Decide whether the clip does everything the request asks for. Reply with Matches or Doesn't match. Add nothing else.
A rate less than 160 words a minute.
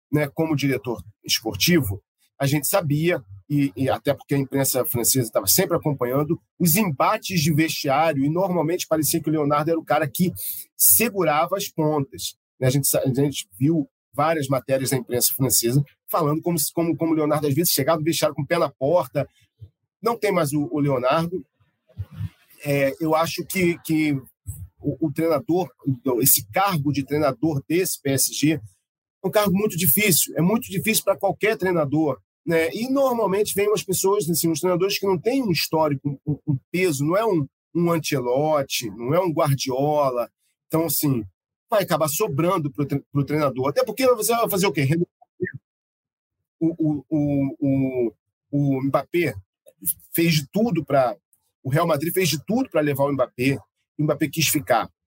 Doesn't match